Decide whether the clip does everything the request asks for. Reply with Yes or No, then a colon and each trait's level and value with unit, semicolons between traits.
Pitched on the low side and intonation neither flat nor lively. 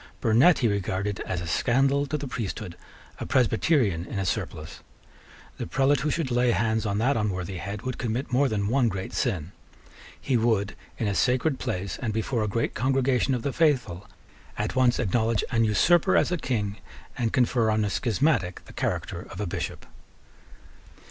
Yes: low, 115 Hz; average, 4.4 semitones